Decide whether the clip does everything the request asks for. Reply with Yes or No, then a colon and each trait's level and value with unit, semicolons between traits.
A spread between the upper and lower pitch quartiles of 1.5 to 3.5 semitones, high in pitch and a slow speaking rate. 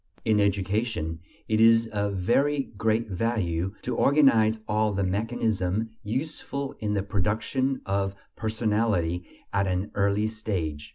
No: narrow, 2.6 semitones; low, 105 Hz; slow, 125 wpm